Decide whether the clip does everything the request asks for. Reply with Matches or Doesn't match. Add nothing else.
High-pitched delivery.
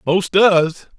Doesn't match